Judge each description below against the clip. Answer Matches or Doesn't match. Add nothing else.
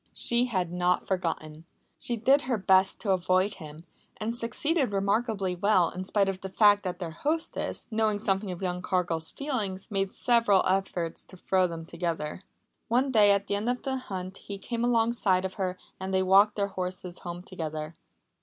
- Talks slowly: Doesn't match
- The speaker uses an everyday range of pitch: Matches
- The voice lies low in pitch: Doesn't match